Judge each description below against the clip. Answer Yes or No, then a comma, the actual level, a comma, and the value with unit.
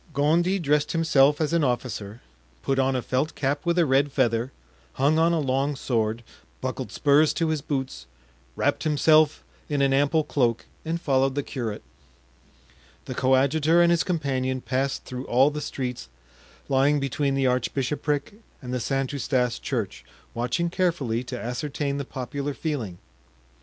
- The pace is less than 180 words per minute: Yes, average, 155 wpm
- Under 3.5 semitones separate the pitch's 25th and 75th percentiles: Yes, average, 2.8 semitones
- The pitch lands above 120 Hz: Yes, medium, 140 Hz